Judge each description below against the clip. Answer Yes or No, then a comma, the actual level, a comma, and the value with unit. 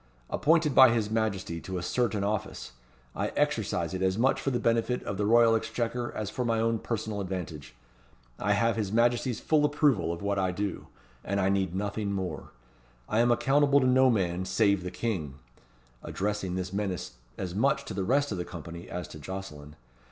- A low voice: Yes, low, 105 Hz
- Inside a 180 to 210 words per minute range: Yes, average, 190 wpm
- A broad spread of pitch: No, average, 4.1 semitones